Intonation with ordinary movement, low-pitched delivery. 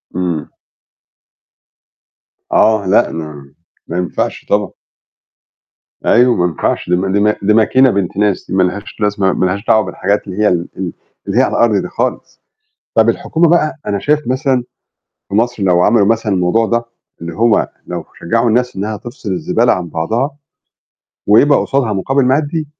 Yes: average, 4.7 semitones; low, 105 Hz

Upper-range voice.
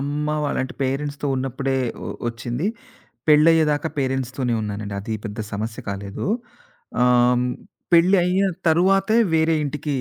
No: medium, 140 Hz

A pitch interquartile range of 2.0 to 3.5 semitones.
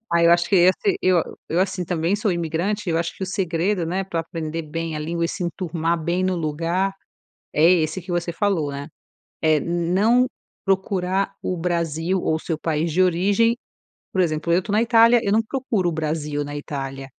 Yes: average, 2.9 semitones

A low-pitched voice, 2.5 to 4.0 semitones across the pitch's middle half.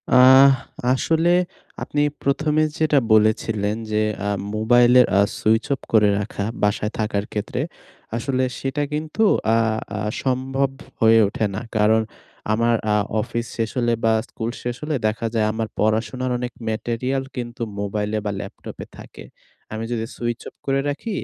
Yes: low, 120 Hz; average, 3.5 semitones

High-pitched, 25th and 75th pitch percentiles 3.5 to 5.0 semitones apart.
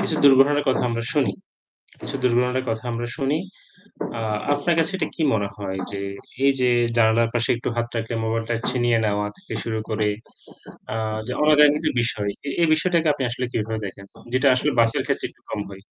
No: low, 120 Hz; average, 4.4 semitones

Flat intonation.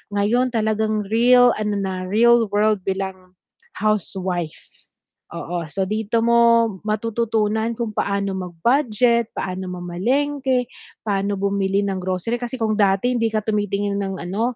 No: average, 3.2 semitones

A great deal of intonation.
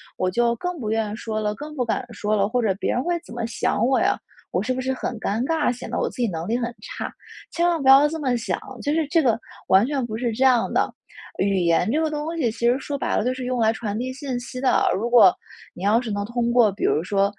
No: average, 3.7 semitones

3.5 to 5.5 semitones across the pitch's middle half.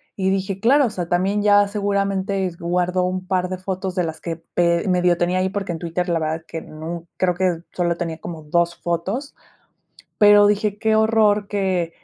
No: average, 2.7 semitones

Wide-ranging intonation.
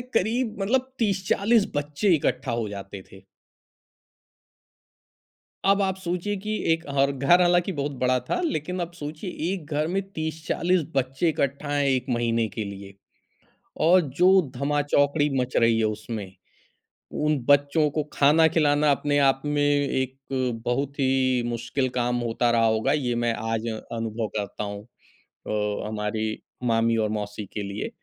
Yes: wide, 5.8 semitones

